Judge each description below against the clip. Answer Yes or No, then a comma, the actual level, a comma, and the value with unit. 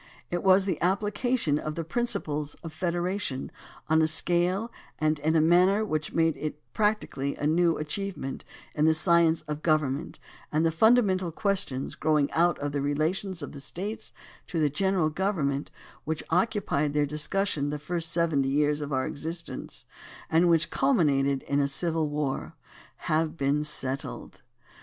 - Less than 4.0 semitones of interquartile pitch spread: Yes, average, 3.6 semitones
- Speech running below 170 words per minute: Yes, average, 160 wpm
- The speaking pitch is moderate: Yes, medium, 160 Hz